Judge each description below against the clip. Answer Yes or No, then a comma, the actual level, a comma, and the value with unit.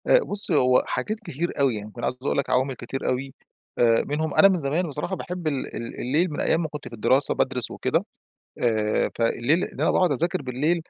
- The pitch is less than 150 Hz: Yes, medium, 140 Hz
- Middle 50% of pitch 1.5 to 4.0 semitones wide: No, average, 5.1 semitones